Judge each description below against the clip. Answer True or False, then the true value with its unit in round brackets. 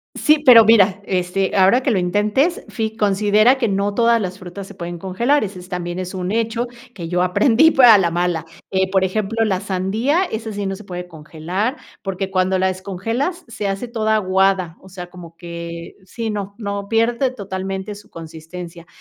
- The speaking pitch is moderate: False (195 Hz)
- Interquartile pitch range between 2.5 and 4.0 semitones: True (3.5 semitones)